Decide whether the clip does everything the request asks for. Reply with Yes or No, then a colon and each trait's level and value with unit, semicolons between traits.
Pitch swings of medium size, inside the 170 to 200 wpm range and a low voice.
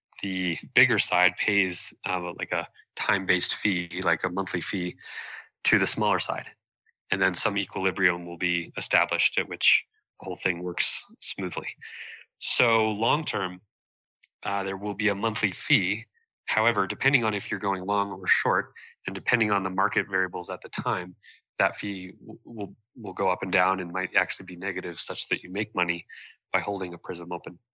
No: narrow, 2.1 semitones; average, 180 wpm; very low, 95 Hz